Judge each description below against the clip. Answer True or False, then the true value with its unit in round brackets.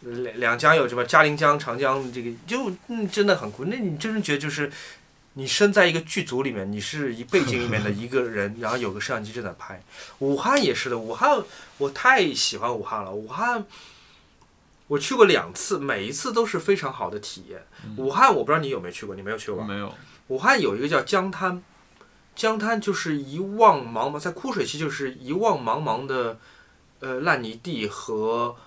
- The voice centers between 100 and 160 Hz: True (140 Hz)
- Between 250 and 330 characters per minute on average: True (290 characters per minute)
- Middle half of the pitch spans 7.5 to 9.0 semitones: True (8.3 semitones)